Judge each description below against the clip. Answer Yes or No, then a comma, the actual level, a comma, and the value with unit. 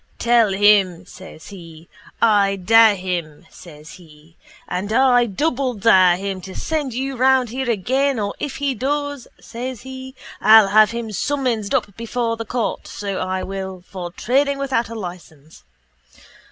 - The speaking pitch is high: Yes, high, 215 Hz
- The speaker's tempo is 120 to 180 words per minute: Yes, average, 150 wpm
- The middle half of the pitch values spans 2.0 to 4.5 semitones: No, wide, 5.4 semitones